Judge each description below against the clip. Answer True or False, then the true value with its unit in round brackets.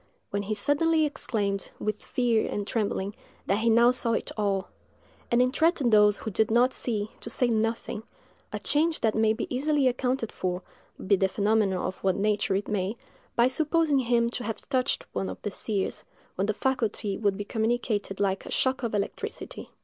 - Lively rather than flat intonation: False (3.6 semitones)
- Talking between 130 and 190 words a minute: True (180 wpm)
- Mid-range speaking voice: False (220 Hz)